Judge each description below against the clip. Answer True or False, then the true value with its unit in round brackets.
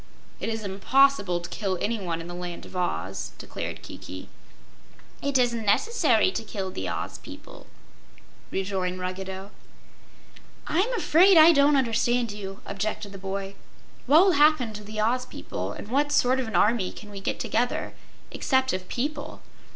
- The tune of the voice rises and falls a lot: True (5.8 semitones)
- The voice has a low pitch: False (220 Hz)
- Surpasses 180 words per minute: False (160 wpm)